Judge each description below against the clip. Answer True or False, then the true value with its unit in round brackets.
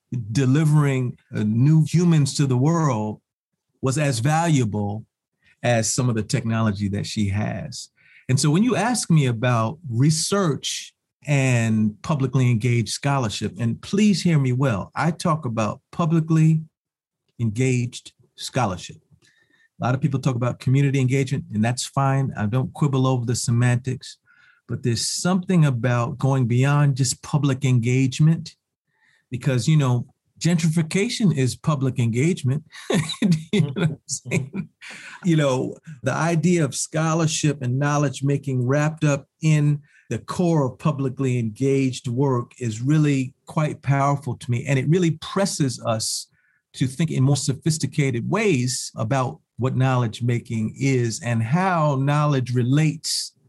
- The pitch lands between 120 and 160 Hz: True (135 Hz)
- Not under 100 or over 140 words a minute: True (135 wpm)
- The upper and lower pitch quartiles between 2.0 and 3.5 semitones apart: False (4.0 semitones)